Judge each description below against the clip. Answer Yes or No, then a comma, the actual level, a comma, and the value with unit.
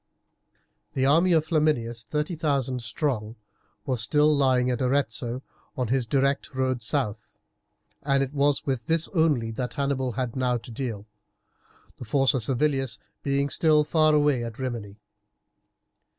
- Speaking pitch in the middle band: No, low, 130 Hz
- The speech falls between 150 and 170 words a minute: No, average, 140 wpm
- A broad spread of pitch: No, average, 3.3 semitones